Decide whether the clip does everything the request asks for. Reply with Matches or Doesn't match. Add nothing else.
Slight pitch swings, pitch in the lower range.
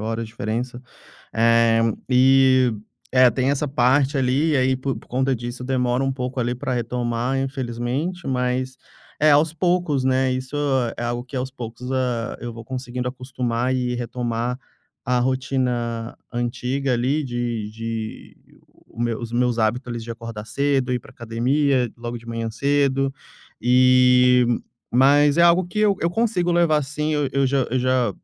Matches